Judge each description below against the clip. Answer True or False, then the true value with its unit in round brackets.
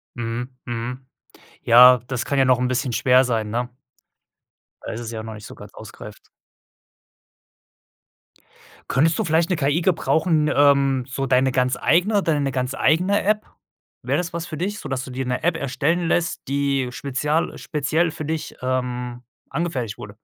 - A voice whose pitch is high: False (135 Hz)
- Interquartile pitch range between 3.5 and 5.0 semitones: True (4.3 semitones)